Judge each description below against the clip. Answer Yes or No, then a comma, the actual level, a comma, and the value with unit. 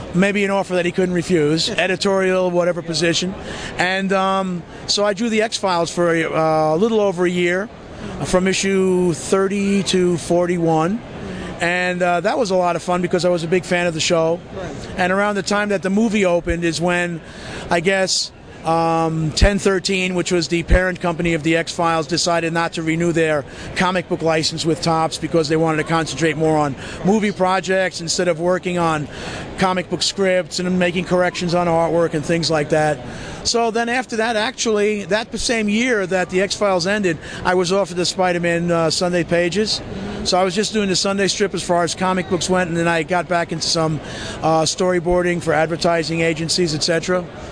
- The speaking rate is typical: Yes, average, 195 wpm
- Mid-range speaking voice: Yes, medium, 180 Hz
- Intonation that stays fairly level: Yes, narrow, 2.3 semitones